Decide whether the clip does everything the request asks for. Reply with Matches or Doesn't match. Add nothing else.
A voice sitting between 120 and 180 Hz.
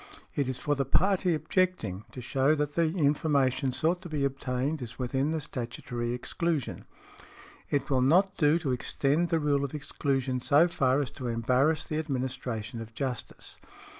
Matches